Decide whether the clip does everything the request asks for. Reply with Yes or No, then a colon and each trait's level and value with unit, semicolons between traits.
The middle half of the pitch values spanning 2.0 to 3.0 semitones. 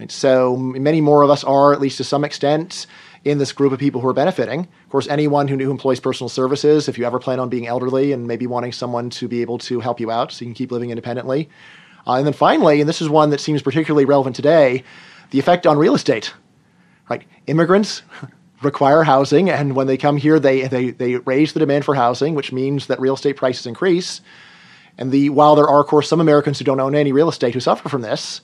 Yes: narrow, 2.5 semitones